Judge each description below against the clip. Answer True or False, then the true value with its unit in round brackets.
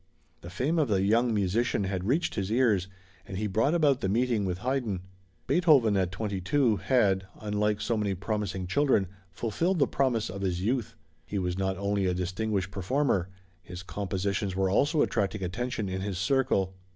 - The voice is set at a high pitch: False (100 Hz)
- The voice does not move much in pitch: False (4.3 semitones)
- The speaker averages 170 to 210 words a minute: True (175 wpm)